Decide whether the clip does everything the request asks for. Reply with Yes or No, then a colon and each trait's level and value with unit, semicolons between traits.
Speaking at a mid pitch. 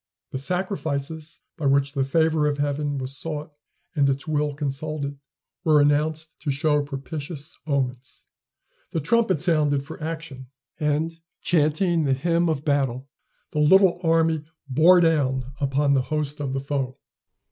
Yes: medium, 150 Hz